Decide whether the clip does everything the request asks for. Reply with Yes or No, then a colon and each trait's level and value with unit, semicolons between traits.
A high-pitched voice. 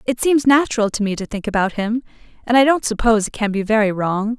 Yes: high, 225 Hz